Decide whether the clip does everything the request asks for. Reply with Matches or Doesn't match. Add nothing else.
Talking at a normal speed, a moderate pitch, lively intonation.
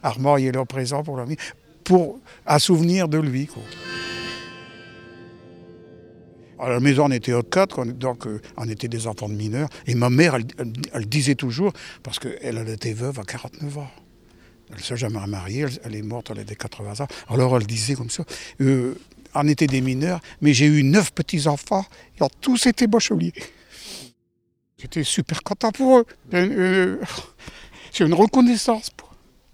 Doesn't match